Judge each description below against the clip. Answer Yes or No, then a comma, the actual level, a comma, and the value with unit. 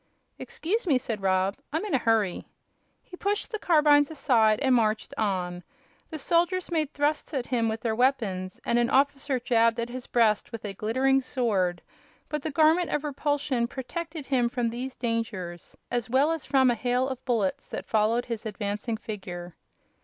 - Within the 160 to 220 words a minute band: Yes, average, 175 wpm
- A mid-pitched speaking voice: No, high, 245 Hz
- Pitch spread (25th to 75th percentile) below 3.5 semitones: No, average, 4.9 semitones